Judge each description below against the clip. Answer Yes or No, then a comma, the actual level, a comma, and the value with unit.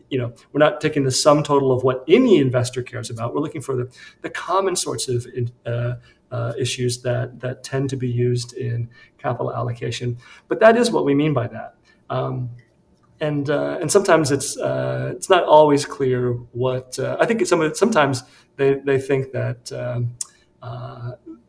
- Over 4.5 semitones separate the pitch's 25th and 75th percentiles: No, average, 2.8 semitones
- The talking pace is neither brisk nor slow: Yes, average, 185 wpm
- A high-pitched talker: No, low, 130 Hz